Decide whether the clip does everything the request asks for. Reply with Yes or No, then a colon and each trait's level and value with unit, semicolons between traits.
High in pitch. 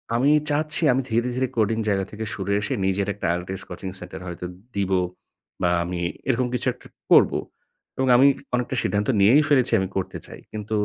No: low, 105 Hz